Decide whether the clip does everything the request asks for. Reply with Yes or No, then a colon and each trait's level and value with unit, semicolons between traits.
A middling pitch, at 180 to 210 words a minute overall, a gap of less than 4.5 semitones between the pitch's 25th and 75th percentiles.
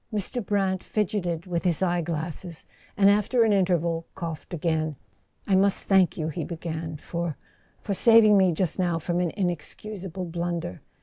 No: medium, 175 Hz; average, 150 wpm; average, 2.8 semitones